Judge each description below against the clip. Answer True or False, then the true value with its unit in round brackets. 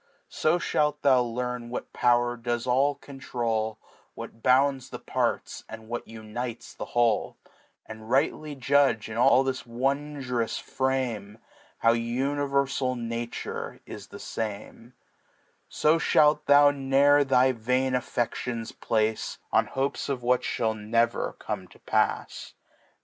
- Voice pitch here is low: True (125 Hz)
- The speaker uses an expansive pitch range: False (2.9 semitones)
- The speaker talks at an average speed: False (125 wpm)